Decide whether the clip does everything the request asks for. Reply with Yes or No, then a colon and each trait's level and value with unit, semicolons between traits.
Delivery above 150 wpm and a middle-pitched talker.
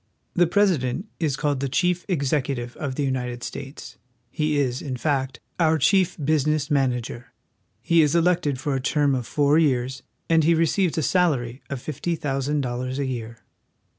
Yes: average, 170 wpm; medium, 145 Hz